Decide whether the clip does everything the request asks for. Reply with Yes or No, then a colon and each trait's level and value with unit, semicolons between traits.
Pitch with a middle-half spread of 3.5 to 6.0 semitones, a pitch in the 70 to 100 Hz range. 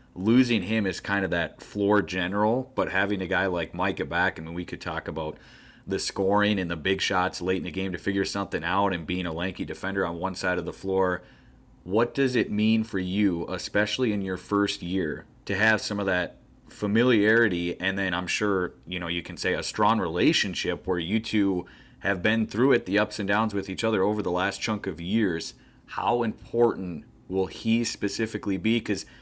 No: narrow, 2.6 semitones; very low, 95 Hz